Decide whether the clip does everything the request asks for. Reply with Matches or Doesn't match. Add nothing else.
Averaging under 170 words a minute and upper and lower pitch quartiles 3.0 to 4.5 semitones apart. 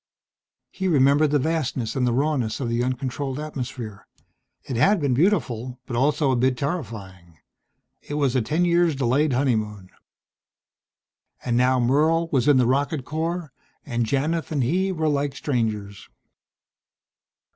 Matches